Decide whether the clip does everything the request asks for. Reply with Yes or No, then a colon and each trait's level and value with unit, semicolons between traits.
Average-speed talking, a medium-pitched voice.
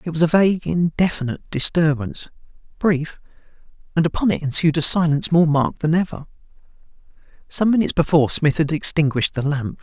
Yes: average, 155 wpm; medium, 160 Hz